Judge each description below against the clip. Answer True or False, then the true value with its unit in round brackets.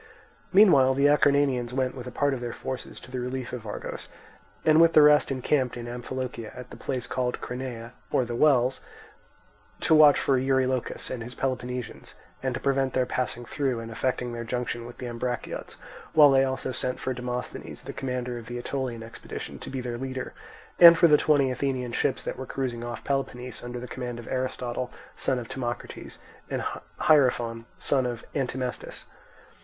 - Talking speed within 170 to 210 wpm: True (180 wpm)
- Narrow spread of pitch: True (1.7 semitones)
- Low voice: True (125 Hz)